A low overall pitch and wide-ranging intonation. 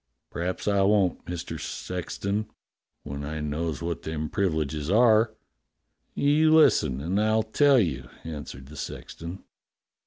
Yes: very low, 90 Hz; wide, 5.7 semitones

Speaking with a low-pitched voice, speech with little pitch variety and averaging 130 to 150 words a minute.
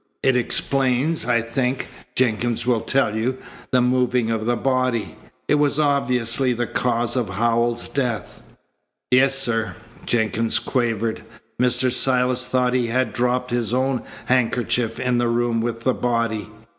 Yes: low, 125 Hz; narrow, 1.7 semitones; average, 145 wpm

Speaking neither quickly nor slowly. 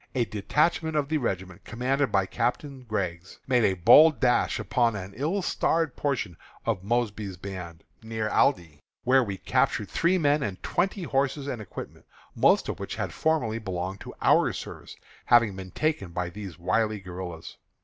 Yes: average, 165 wpm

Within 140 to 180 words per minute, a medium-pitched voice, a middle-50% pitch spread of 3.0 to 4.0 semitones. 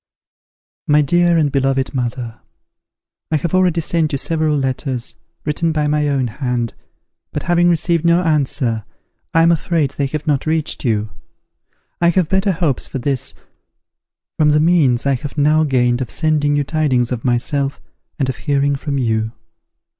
Yes: average, 160 wpm; medium, 145 Hz; average, 3.5 semitones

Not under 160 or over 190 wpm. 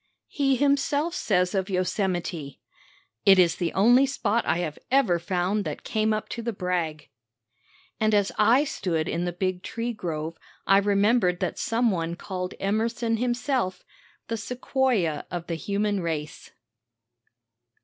No: average, 145 wpm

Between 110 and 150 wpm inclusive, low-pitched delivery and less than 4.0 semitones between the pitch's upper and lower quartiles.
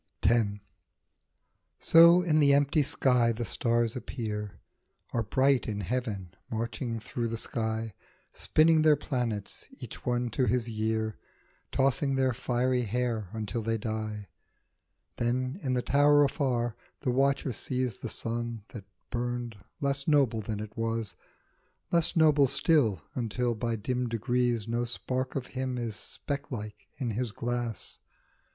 Yes: slow, 135 wpm; low, 120 Hz; average, 2.9 semitones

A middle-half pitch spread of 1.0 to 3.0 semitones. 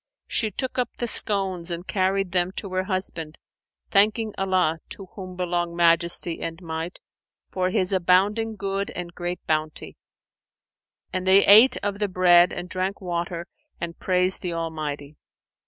Yes: narrow, 2.4 semitones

